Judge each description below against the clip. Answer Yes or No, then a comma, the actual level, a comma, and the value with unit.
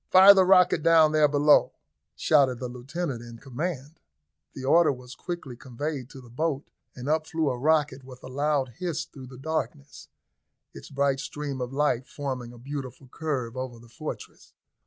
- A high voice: No, medium, 140 Hz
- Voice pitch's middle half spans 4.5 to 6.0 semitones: No, average, 3.6 semitones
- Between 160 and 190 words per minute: Yes, average, 175 wpm